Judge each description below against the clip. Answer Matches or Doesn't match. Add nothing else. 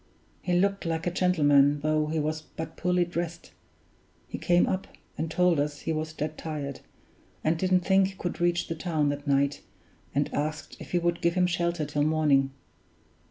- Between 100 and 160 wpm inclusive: Doesn't match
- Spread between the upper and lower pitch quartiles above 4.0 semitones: Doesn't match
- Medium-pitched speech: Matches